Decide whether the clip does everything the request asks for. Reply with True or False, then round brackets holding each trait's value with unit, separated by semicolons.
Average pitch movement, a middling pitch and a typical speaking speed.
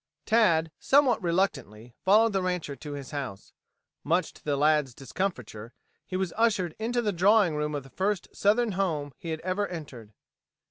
False (5.8 semitones; 170 Hz; 170 wpm)